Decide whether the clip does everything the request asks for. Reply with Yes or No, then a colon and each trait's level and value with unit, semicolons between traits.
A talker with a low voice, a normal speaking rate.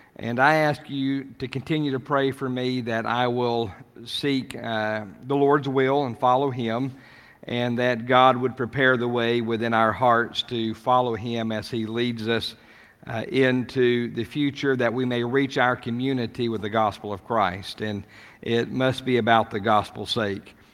Yes: low, 120 Hz; average, 175 wpm